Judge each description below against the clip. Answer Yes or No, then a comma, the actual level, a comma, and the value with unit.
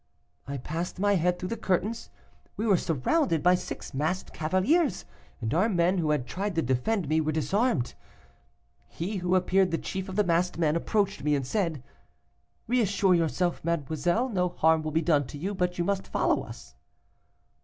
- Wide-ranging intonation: No, average, 3.8 semitones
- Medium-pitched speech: Yes, medium, 175 Hz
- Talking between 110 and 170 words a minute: No, average, 180 wpm